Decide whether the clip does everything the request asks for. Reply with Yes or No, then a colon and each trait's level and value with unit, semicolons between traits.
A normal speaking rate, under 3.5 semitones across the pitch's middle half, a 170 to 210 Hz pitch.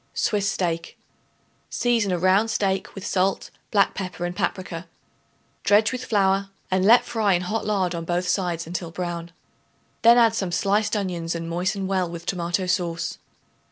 Yes: average, 160 wpm; average, 2.7 semitones; medium, 185 Hz